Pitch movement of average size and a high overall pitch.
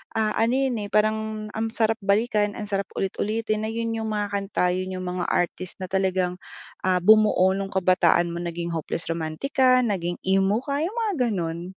Yes: average, 3.3 semitones; high, 200 Hz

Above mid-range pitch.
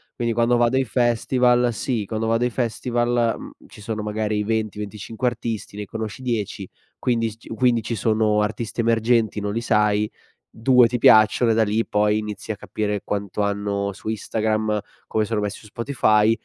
No: low, 110 Hz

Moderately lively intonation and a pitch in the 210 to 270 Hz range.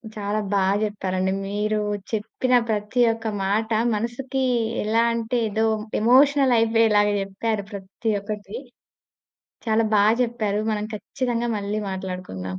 No: narrow, 2.3 semitones; high, 215 Hz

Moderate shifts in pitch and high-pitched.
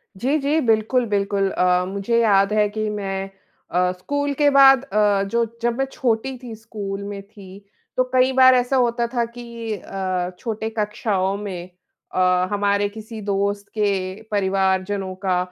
Yes: average, 3.3 semitones; high, 210 Hz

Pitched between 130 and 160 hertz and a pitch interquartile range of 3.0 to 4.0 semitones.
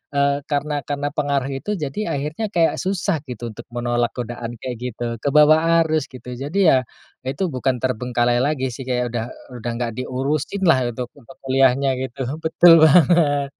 Yes: low, 135 Hz; average, 3.4 semitones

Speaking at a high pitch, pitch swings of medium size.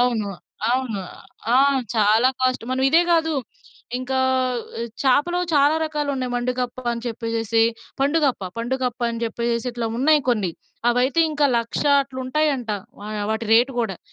Yes: very high, 250 Hz; average, 3.2 semitones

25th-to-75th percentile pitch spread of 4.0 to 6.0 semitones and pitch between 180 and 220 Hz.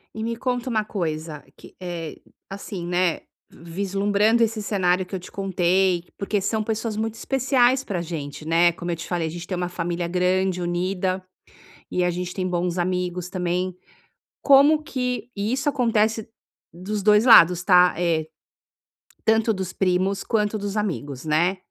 No: average, 3.6 semitones; medium, 185 Hz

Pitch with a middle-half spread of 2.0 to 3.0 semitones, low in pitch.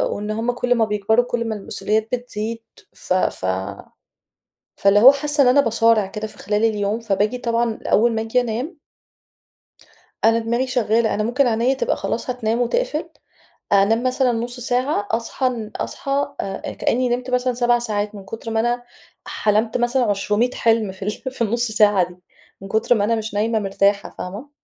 No: average, 2.7 semitones; high, 230 Hz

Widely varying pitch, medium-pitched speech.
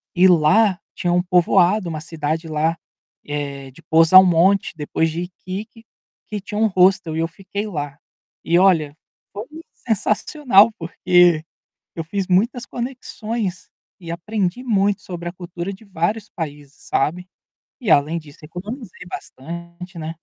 No: average, 3.6 semitones; medium, 180 Hz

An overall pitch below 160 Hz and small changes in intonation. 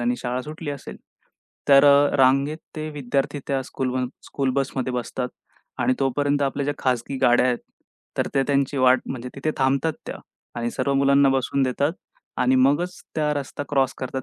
Yes: low, 135 Hz; narrow, 1.8 semitones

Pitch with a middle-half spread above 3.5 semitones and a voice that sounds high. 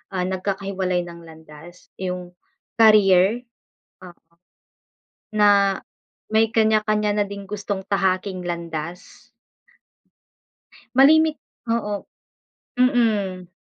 No: average, 2.7 semitones; high, 195 Hz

